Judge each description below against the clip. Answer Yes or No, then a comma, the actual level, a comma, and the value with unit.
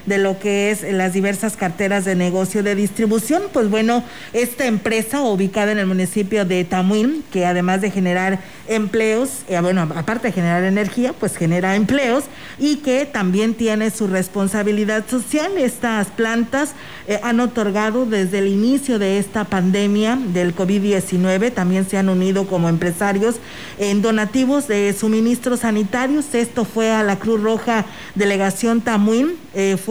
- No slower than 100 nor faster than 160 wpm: Yes, average, 155 wpm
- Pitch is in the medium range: No, high, 210 Hz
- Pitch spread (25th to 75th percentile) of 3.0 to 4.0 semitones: Yes, average, 3.3 semitones